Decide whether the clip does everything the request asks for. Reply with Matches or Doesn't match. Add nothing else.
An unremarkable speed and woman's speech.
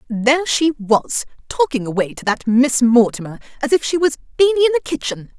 Matches